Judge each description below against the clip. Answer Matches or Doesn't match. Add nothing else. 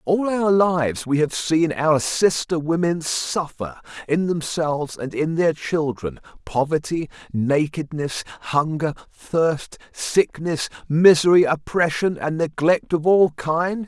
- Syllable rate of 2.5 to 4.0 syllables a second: Matches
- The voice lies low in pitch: Doesn't match